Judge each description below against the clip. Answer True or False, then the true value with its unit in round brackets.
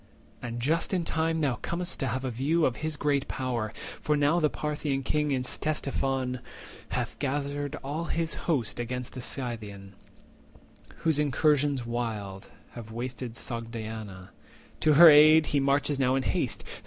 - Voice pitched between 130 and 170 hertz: True (135 Hz)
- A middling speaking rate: True (155 wpm)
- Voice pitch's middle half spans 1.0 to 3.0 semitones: False (3.9 semitones)